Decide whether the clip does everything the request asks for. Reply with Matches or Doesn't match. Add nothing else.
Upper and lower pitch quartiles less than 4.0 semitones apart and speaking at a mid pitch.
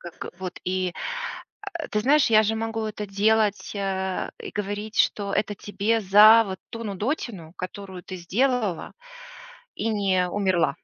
Doesn't match